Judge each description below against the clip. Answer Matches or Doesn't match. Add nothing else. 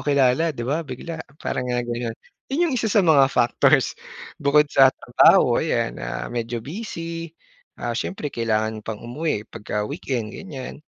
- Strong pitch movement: Matches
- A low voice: Matches